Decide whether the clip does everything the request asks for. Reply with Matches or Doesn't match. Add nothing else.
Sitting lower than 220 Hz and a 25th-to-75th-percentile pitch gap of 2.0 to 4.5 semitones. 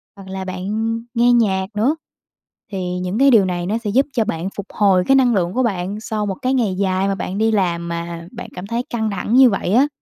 Matches